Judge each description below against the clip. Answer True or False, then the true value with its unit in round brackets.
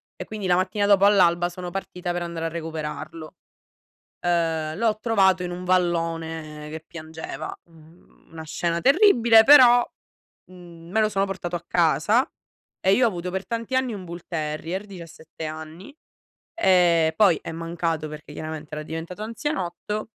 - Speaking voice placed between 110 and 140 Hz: False (175 Hz)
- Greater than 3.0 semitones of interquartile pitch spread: True (3.6 semitones)